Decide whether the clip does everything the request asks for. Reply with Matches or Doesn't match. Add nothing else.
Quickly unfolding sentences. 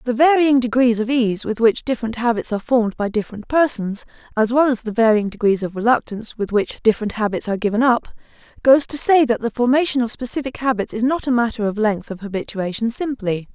Matches